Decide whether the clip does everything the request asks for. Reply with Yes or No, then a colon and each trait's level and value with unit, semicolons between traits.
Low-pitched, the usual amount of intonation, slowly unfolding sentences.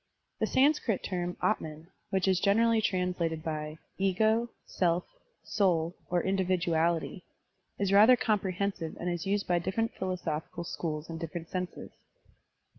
No: medium, 180 Hz; average, 3.1 semitones; slow, 130 wpm